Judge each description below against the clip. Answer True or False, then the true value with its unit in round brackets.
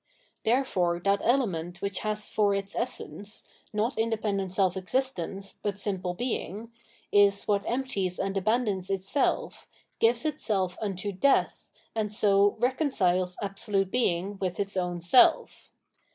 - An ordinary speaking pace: False (130 wpm)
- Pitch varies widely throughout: False (3.1 semitones)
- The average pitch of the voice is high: True (200 Hz)